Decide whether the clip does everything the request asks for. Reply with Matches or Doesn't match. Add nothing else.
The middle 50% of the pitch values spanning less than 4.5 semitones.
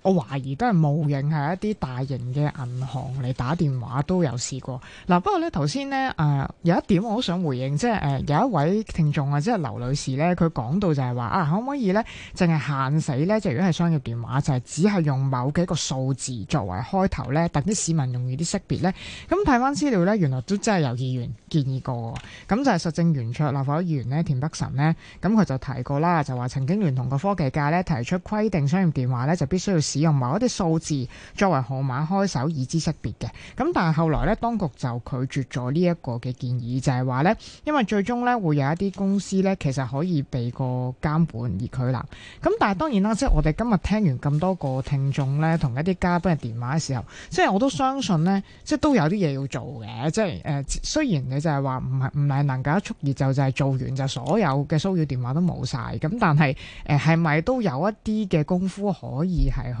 Doesn't match